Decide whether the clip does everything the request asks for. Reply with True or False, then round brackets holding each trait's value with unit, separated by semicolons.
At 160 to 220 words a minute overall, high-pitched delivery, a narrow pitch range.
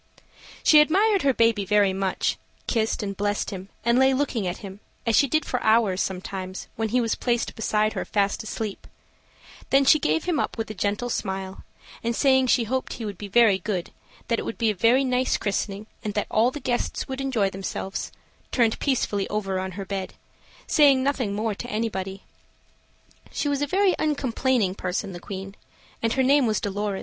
False (190 wpm; 220 Hz; 4.7 semitones)